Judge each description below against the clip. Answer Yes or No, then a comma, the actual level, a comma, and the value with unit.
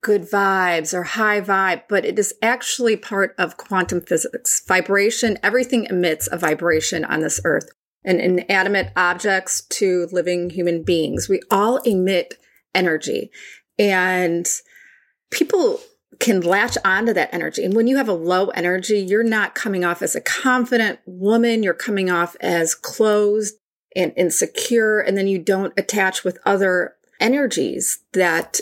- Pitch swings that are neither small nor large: Yes, average, 3.8 semitones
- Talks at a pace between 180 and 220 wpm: No, average, 150 wpm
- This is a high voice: Yes, high, 195 Hz